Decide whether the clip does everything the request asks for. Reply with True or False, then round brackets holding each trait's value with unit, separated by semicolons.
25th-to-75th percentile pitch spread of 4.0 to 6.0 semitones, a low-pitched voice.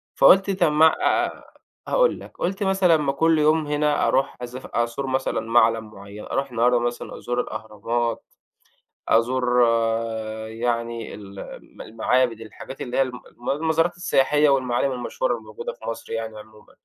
True (4.7 semitones; 125 Hz)